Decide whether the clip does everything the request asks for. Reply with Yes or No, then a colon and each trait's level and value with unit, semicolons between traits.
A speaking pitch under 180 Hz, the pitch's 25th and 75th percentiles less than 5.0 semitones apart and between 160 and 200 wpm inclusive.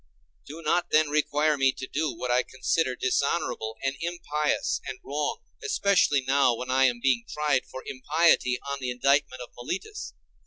Yes: medium, 140 Hz; average, 3.3 semitones; average, 165 wpm